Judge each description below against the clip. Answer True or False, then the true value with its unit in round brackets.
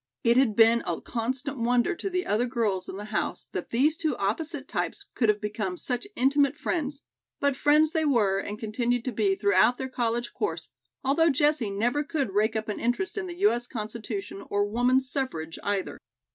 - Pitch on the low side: False (240 Hz)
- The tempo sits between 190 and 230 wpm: True (195 wpm)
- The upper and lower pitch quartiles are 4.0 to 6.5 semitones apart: True (5.1 semitones)